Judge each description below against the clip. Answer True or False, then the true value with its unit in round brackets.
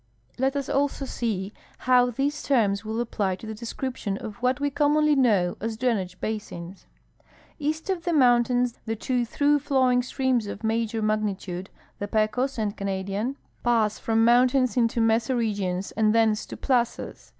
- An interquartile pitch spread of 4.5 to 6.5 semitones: False (3.5 semitones)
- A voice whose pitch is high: True (230 Hz)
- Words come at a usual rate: True (160 wpm)